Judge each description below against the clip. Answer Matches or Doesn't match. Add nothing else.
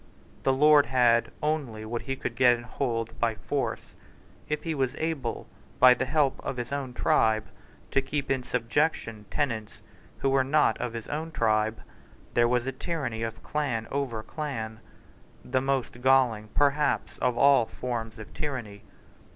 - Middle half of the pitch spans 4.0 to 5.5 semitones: Doesn't match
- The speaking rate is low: Doesn't match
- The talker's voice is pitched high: Doesn't match